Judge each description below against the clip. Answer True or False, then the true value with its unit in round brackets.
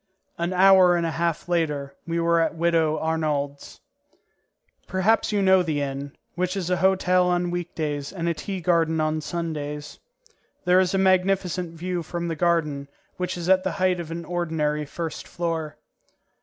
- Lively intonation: False (2.4 semitones)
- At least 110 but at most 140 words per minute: False (170 wpm)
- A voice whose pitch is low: False (170 Hz)